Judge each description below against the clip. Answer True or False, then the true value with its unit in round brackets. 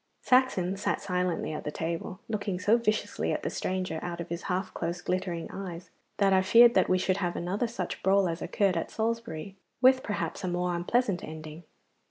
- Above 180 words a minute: True (195 wpm)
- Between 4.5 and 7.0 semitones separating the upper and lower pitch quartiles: False (3.1 semitones)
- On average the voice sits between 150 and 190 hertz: True (185 Hz)